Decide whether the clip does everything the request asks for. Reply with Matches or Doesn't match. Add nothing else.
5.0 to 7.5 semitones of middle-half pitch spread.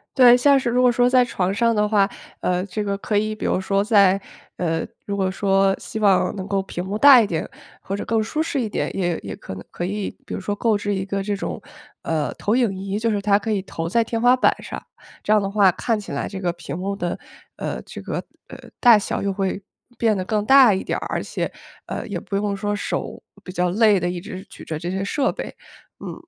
Doesn't match